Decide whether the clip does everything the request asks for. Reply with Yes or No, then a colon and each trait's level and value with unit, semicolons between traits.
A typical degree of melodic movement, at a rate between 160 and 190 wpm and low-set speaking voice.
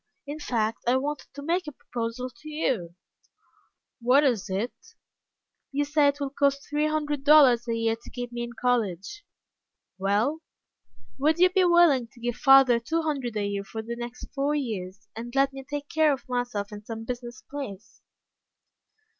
No: average, 4.2 semitones; average, 175 wpm; very high, 250 Hz